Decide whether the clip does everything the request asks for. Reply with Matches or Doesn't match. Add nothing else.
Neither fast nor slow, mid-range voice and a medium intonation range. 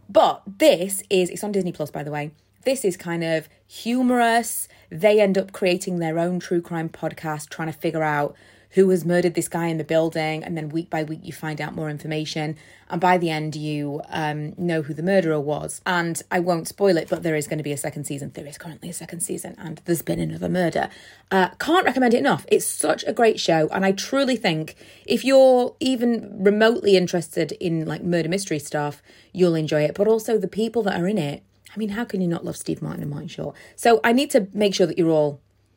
Doesn't match